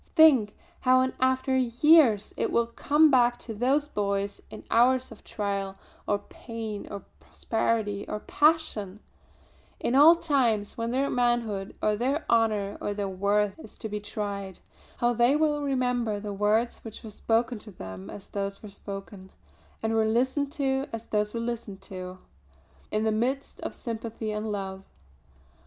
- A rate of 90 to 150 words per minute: No, average, 160 wpm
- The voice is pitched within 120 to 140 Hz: No, high, 225 Hz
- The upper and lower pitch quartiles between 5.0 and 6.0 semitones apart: No, average, 3.8 semitones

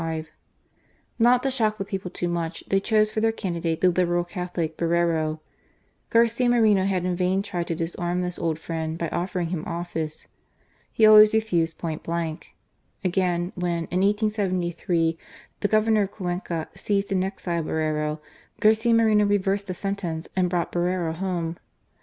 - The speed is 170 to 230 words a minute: No, average, 155 wpm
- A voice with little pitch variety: No, average, 3.2 semitones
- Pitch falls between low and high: Yes, medium, 180 Hz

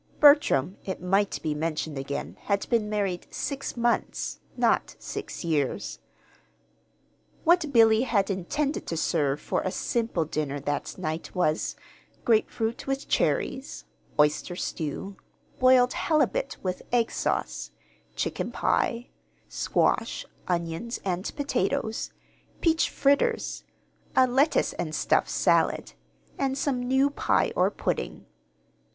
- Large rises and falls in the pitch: Yes, wide, 8.1 semitones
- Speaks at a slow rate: Yes, slow, 115 wpm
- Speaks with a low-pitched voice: No, high, 220 Hz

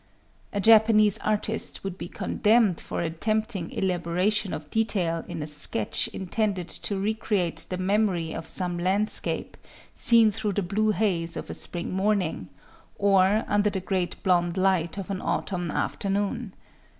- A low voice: No, high, 195 Hz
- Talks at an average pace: Yes, average, 150 wpm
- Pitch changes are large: No, average, 3.3 semitones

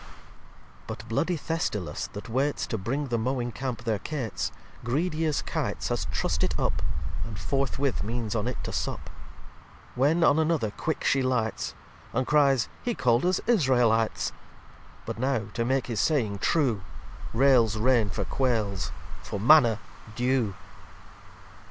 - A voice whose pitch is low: Yes, low, 125 Hz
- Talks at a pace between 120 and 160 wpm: Yes, average, 145 wpm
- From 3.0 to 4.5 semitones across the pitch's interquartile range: Yes, average, 4.0 semitones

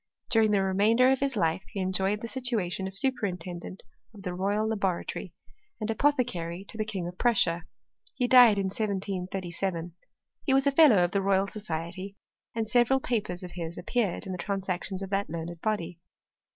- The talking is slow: No, average, 175 wpm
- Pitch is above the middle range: Yes, high, 195 Hz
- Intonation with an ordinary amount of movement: Yes, average, 3.7 semitones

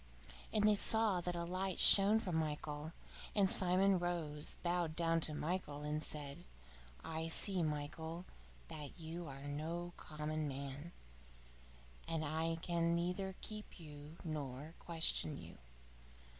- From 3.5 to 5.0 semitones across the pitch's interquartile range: No, average, 2.9 semitones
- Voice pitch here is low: No, medium, 165 Hz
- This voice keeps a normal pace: No, slow, 130 wpm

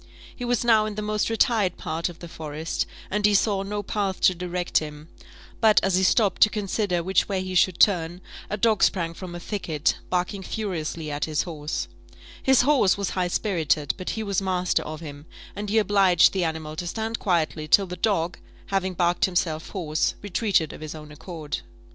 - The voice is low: No, medium, 185 Hz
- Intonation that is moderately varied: Yes, average, 4.0 semitones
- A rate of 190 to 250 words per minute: Yes, average, 195 wpm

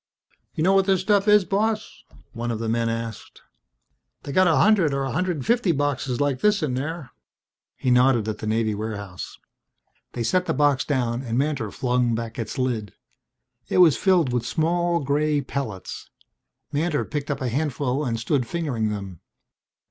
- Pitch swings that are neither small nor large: No, wide, 6.0 semitones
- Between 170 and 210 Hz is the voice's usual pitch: No, low, 135 Hz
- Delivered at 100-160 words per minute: No, average, 175 wpm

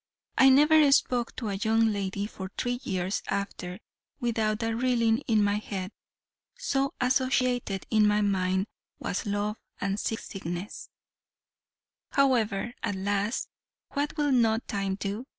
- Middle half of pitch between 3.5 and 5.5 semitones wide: Yes, average, 3.8 semitones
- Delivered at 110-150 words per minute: Yes, slow, 135 wpm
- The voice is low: No, high, 215 Hz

